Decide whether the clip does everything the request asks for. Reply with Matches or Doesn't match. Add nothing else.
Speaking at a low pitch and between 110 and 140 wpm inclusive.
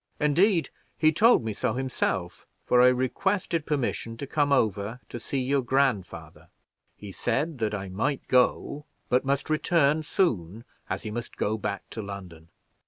Doesn't match